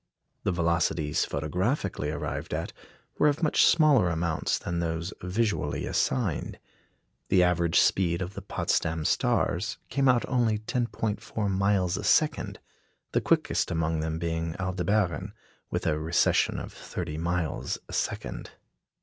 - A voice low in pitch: Yes, very low, 90 Hz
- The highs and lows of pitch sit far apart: No, average, 4.1 semitones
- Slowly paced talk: Yes, slow, 130 wpm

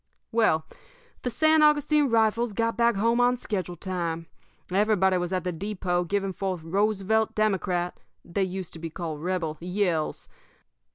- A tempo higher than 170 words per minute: No, average, 150 wpm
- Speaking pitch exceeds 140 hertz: Yes, high, 190 Hz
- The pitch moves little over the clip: No, average, 3.9 semitones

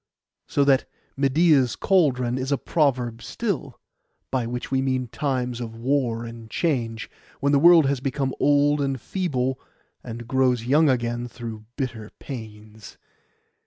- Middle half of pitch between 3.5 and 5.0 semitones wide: No, average, 3.1 semitones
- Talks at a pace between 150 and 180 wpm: No, average, 140 wpm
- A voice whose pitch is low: Yes, low, 130 Hz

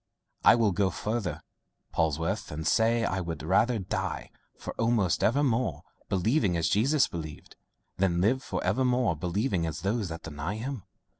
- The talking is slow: No, average, 145 wpm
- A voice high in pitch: No, very low, 95 Hz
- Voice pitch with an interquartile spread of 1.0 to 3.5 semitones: No, wide, 5.6 semitones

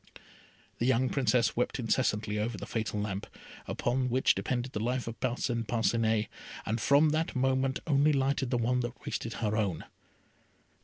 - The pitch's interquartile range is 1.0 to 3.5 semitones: Yes, average, 2.8 semitones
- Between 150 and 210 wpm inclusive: Yes, average, 160 wpm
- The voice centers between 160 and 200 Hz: No, low, 120 Hz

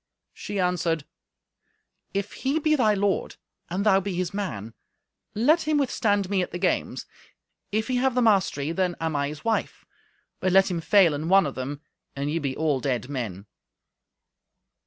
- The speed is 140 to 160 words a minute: No, average, 175 wpm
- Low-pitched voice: No, medium, 185 Hz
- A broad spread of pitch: Yes, wide, 5.8 semitones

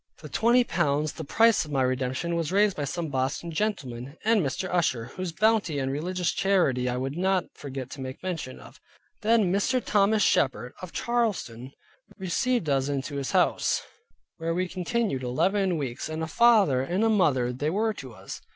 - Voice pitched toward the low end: No, medium, 165 Hz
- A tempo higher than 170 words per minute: Yes, average, 180 wpm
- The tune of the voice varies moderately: No, wide, 6.8 semitones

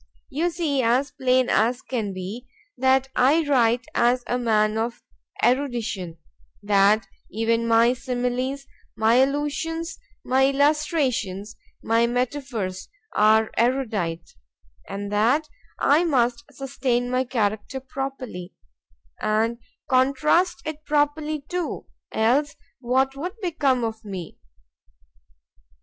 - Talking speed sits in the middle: No, slow, 100 wpm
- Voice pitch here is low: No, very high, 250 Hz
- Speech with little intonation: No, average, 4.1 semitones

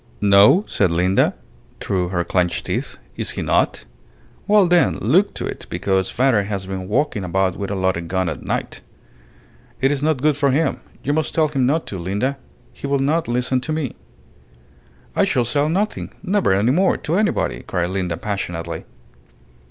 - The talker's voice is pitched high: No, low, 115 Hz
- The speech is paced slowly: No, average, 175 wpm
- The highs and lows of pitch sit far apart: Yes, wide, 8.0 semitones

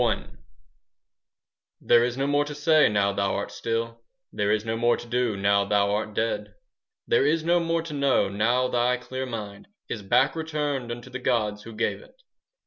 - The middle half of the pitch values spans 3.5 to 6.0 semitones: Yes, average, 5.1 semitones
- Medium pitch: No, low, 120 Hz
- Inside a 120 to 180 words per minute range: No, average, 190 wpm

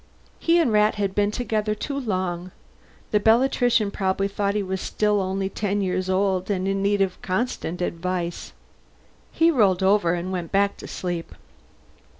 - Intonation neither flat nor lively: No, narrow, 2.2 semitones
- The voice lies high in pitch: Yes, high, 195 Hz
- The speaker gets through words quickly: No, average, 160 wpm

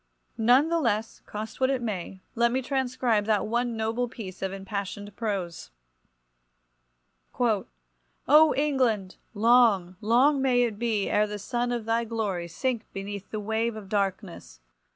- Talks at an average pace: Yes, average, 145 wpm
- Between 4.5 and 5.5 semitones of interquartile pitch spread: No, average, 3.5 semitones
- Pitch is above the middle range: Yes, high, 220 Hz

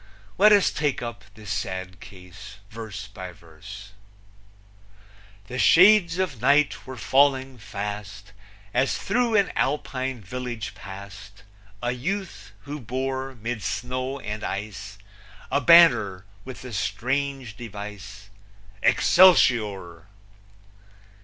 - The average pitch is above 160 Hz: No, low, 115 Hz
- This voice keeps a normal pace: No, slow, 105 wpm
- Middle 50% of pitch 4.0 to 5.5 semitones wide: Yes, average, 5.1 semitones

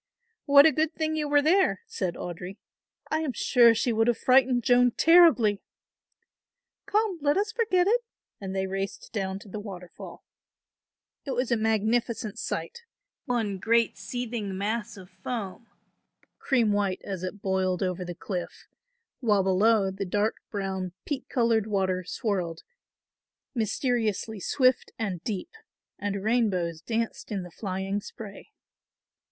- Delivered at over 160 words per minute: No, average, 140 wpm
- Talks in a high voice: Yes, high, 215 Hz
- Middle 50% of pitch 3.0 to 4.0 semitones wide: No, average, 4.5 semitones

